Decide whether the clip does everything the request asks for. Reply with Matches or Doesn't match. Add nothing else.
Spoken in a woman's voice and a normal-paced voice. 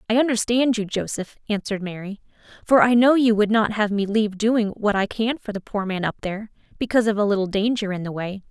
Doesn't match